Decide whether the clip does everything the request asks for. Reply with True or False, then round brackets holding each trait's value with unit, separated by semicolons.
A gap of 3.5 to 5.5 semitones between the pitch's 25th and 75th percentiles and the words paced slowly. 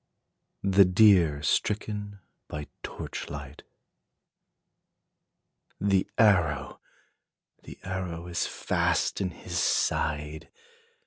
True (4.9 semitones; 80 wpm)